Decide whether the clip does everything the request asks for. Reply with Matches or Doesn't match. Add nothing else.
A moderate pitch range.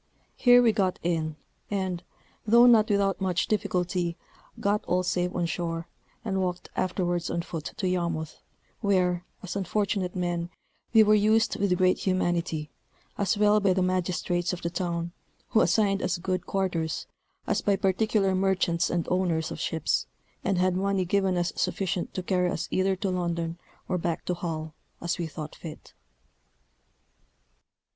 Doesn't match